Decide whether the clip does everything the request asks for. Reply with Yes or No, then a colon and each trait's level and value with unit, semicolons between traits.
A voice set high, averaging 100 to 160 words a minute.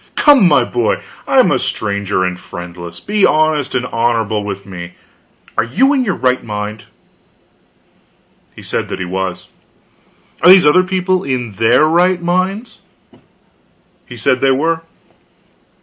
No: low, 125 Hz; average, 140 wpm